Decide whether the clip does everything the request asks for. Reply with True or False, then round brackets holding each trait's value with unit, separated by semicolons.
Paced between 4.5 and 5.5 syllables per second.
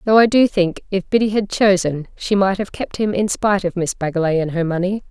False (5.7 syllables/s)